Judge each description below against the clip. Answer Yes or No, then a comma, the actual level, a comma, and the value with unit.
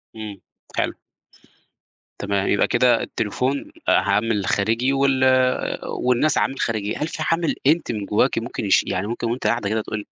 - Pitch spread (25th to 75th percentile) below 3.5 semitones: No, average, 4.3 semitones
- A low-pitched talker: Yes, low, 115 Hz